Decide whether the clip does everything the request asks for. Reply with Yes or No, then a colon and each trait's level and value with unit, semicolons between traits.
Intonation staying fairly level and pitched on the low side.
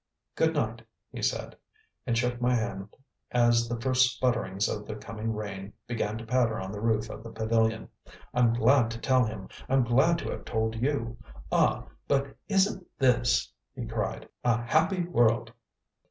Yes: narrow, 2.3 semitones; low, 115 Hz